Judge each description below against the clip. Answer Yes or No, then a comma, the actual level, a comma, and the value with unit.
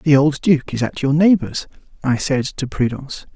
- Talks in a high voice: No, medium, 140 Hz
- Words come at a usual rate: Yes, average, 195 wpm